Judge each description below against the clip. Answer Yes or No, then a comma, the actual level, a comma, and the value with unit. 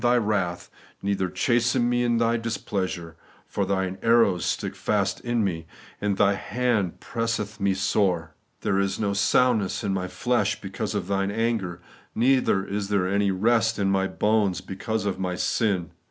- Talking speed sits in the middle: Yes, average, 165 wpm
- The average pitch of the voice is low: Yes, low, 100 Hz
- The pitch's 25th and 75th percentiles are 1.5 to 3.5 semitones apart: Yes, average, 3.1 semitones